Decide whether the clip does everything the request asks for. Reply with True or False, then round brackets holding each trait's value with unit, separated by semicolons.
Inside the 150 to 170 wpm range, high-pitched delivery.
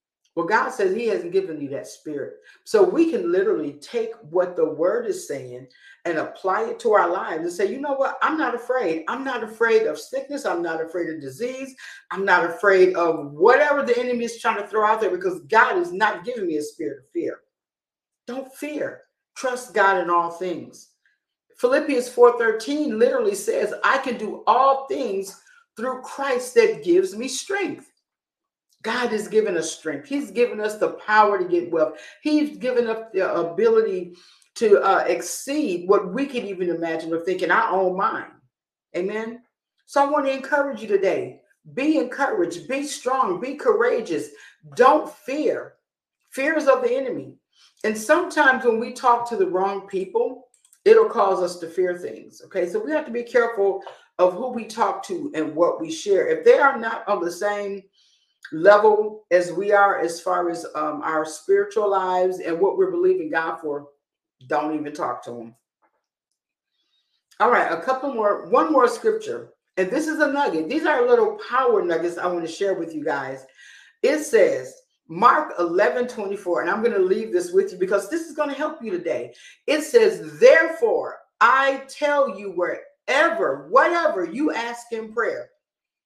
False (180 wpm; 245 Hz)